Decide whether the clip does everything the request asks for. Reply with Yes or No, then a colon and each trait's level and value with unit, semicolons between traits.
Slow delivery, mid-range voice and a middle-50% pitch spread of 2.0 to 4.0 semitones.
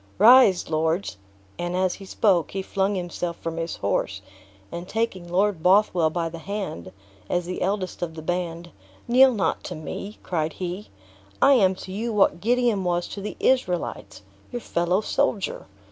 No: average, 165 wpm; medium, 180 Hz; average, 3.3 semitones